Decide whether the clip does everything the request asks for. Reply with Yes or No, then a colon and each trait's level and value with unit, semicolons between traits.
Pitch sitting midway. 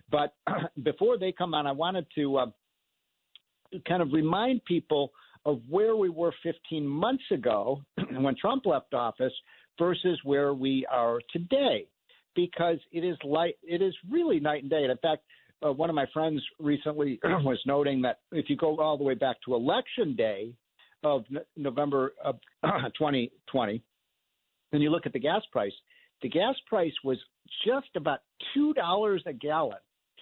Yes: medium, 155 Hz